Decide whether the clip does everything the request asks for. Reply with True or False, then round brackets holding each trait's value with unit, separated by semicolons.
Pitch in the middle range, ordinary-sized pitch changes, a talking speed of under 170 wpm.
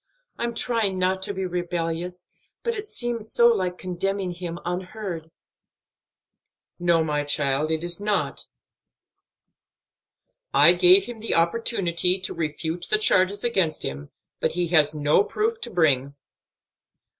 True (180 Hz; 4.2 semitones; 135 wpm)